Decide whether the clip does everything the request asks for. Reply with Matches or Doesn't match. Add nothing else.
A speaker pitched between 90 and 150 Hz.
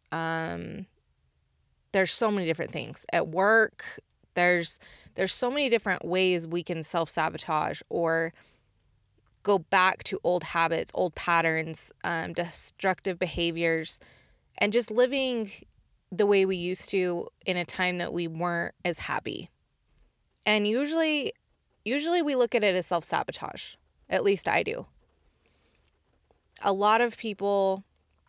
Doesn't match